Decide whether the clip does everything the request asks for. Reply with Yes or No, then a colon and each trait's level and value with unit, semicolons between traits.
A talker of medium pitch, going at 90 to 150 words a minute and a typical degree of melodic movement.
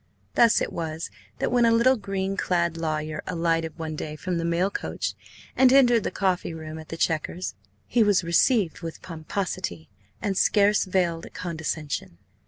No: medium, 170 Hz; average, 165 wpm; average, 3.8 semitones